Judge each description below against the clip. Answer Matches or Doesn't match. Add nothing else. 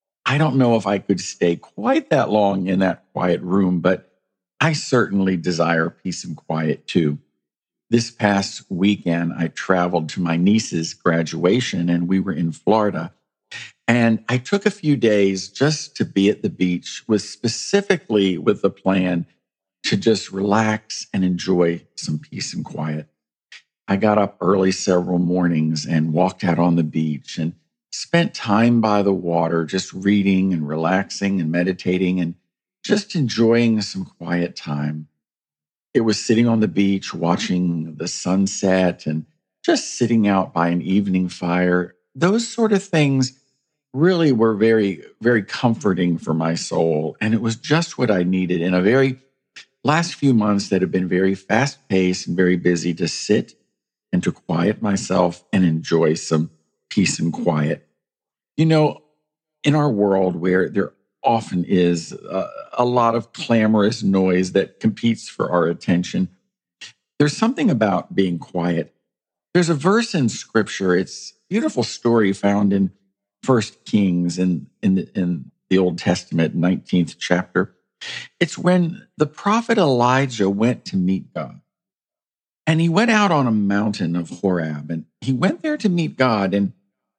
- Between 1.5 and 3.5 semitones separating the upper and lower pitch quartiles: Doesn't match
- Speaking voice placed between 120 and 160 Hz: Doesn't match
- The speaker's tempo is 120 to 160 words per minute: Matches